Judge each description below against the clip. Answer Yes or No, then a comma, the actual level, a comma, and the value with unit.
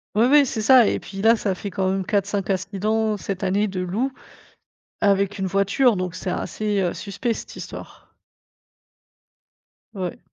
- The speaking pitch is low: No, high, 200 Hz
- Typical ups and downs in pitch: No, narrow, 2.3 semitones